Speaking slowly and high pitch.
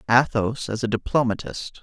No: slow, 130 wpm; low, 115 Hz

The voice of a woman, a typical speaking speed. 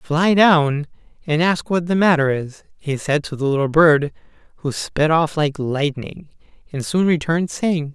No: male; average, 175 wpm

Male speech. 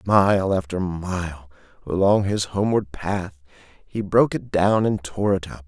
Yes: male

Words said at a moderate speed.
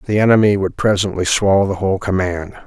Yes: average, 180 wpm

